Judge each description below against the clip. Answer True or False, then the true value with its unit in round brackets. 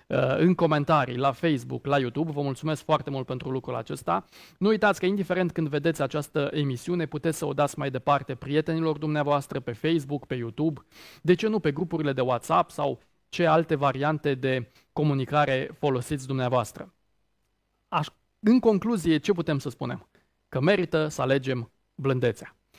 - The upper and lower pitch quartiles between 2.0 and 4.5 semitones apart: True (3.6 semitones)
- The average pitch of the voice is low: False (145 Hz)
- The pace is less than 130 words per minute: False (160 wpm)